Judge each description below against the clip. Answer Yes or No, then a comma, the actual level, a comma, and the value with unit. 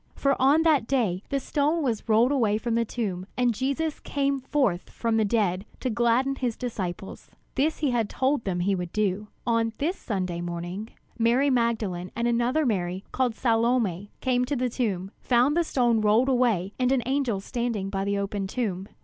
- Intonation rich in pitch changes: No, average, 4.6 semitones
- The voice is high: Yes, high, 235 Hz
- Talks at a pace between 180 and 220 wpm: Yes, average, 185 wpm